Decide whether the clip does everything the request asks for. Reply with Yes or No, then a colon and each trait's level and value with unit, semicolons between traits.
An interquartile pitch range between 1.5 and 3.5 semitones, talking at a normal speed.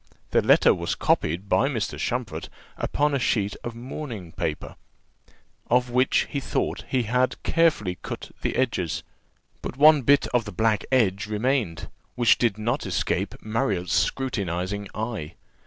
No: average, 4.4 semitones; average, 150 wpm